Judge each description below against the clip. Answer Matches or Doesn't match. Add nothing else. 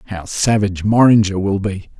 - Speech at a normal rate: Matches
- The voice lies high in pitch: Doesn't match